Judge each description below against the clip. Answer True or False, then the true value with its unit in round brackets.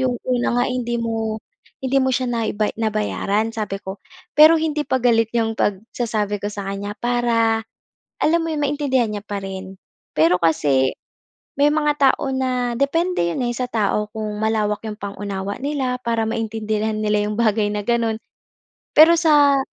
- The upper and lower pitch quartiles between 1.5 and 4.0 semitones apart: True (3.6 semitones)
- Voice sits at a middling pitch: False (225 Hz)